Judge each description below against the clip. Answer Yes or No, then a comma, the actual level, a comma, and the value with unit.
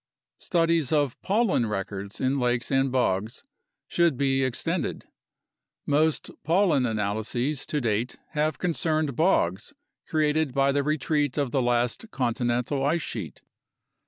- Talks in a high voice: No, low, 135 Hz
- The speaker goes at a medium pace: No, slow, 125 wpm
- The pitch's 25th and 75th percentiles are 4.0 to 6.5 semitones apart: Yes, average, 4.4 semitones